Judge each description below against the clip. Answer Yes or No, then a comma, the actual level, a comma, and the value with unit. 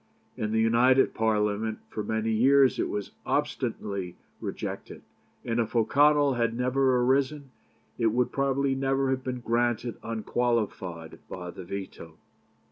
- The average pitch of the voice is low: Yes, low, 120 Hz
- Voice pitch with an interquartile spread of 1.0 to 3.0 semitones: No, average, 3.5 semitones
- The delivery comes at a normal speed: No, slow, 130 wpm